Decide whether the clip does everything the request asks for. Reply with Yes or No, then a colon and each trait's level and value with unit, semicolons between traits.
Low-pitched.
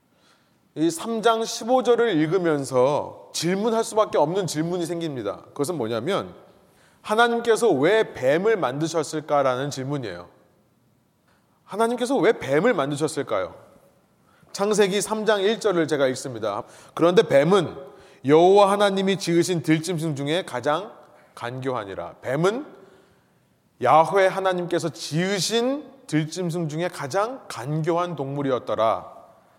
No: medium, 175 Hz